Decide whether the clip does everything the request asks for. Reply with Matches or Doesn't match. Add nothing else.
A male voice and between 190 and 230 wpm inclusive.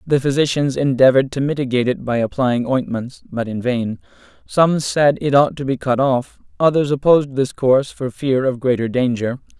Doesn't match